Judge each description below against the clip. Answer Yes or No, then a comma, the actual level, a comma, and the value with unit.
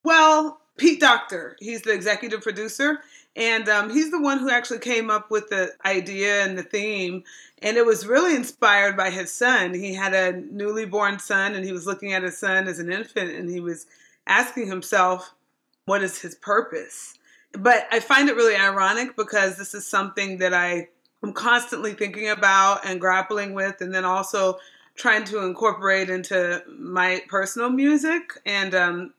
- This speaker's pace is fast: No, average, 175 wpm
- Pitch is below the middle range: No, high, 200 Hz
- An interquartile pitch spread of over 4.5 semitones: No, average, 3.8 semitones